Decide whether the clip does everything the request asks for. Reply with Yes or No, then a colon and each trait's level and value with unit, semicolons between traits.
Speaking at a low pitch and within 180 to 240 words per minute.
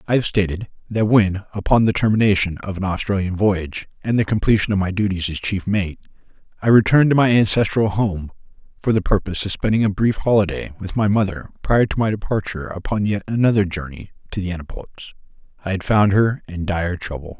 Yes: low, 100 Hz; average, 195 wpm